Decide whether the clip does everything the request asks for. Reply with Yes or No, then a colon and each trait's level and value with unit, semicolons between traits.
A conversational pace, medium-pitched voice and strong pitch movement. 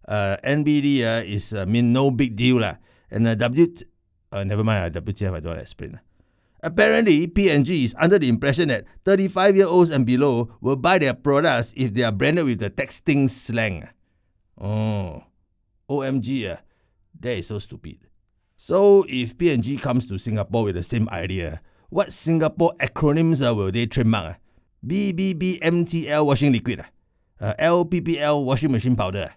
No: average, 165 wpm; low, 120 Hz; wide, 6.6 semitones